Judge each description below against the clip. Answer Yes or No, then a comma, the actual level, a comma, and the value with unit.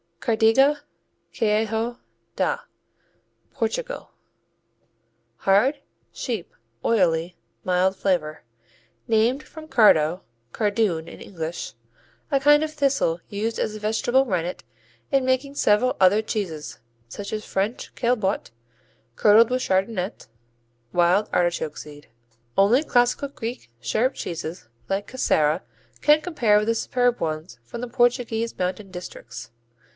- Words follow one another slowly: Yes, slow, 115 wpm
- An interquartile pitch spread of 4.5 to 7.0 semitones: Yes, wide, 5.5 semitones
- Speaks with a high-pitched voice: Yes, high, 215 Hz